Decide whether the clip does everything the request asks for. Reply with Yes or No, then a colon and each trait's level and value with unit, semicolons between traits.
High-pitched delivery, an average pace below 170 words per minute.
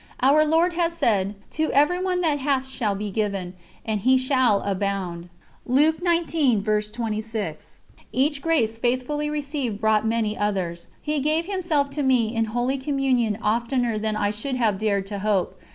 Yes: high, 245 Hz; average, 145 wpm